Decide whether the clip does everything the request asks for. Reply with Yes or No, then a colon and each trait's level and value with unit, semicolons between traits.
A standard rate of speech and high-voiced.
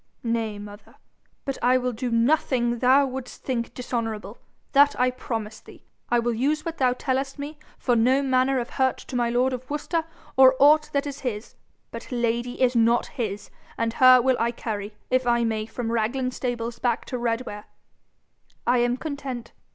Yes: average, 180 wpm; high, 245 Hz